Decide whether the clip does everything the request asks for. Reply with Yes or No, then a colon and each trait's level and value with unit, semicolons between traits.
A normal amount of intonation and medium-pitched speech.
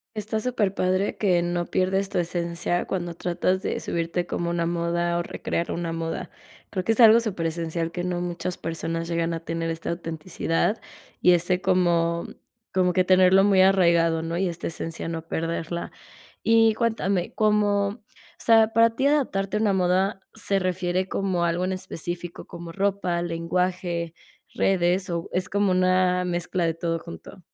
No: narrow, 2.3 semitones; medium, 180 Hz